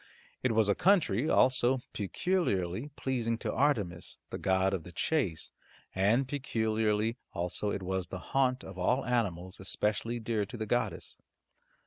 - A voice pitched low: Yes, low, 110 Hz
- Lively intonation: No, average, 5.0 semitones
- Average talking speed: Yes, average, 145 wpm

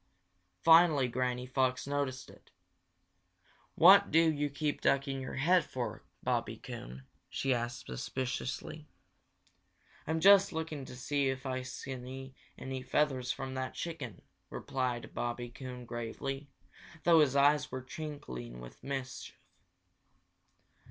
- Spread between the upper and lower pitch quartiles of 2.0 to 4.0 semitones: Yes, narrow, 2.6 semitones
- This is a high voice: No, low, 130 Hz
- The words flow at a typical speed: No, slow, 125 wpm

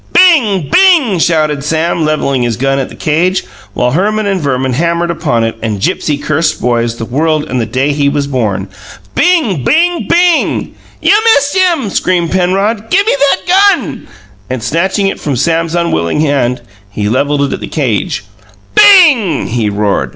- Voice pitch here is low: No, medium, 160 Hz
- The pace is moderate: Yes, average, 170 wpm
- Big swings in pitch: Yes, wide, 8.5 semitones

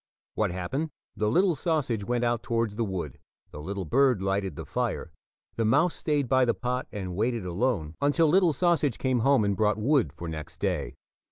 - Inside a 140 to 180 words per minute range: No, average, 190 wpm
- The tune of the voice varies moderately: No, wide, 6.1 semitones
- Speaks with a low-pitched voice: Yes, low, 115 Hz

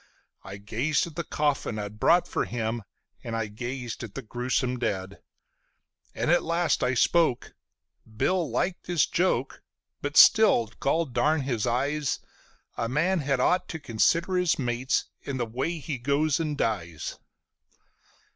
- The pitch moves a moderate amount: No, wide, 5.7 semitones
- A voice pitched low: Yes, low, 130 Hz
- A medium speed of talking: Yes, average, 145 wpm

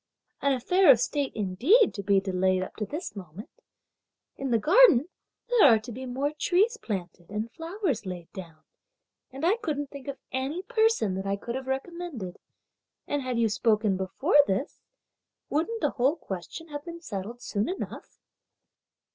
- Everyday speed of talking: Yes, average, 165 wpm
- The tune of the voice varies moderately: No, wide, 8.4 semitones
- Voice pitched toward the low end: No, very high, 260 Hz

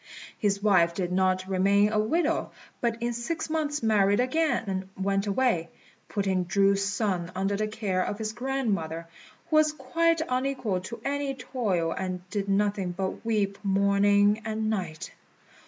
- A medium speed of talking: Yes, average, 155 wpm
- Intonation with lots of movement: No, average, 3.9 semitones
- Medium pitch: No, high, 205 Hz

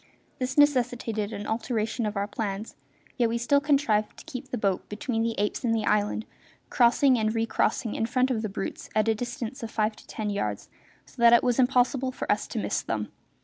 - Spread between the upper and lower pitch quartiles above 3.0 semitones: No, narrow, 2.6 semitones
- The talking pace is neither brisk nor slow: No, fast, 210 wpm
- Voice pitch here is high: Yes, high, 230 Hz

